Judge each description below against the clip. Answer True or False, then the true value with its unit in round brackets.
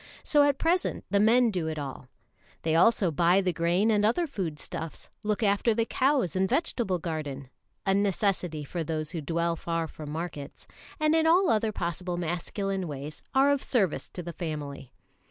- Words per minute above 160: True (180 wpm)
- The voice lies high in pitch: False (180 Hz)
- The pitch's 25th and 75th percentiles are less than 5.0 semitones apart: False (5.6 semitones)